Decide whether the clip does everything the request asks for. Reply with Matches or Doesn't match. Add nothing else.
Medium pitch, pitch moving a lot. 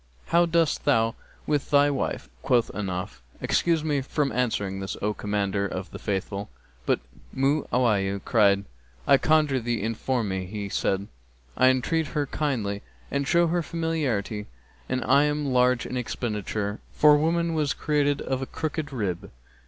Doesn't match